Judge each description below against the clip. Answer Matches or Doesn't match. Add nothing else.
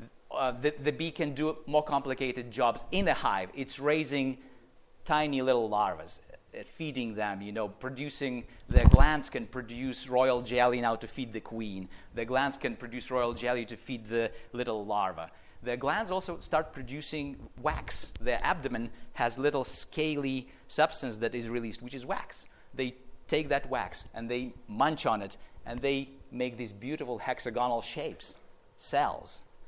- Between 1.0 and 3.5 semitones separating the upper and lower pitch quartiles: Matches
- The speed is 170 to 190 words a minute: Doesn't match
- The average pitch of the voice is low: Matches